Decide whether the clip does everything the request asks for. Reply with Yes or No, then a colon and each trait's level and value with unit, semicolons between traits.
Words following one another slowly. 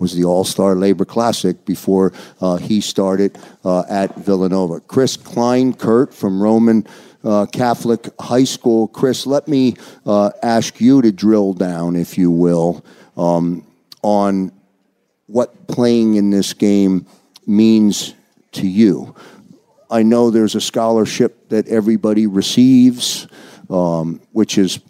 Yes: slow, 130 wpm